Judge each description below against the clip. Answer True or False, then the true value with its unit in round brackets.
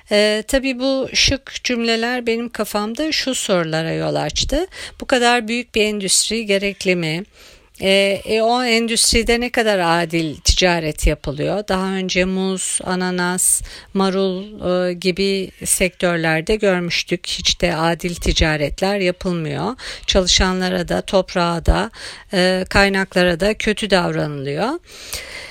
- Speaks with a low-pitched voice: False (195 Hz)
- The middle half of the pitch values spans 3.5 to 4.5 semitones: True (4.1 semitones)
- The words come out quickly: False (120 wpm)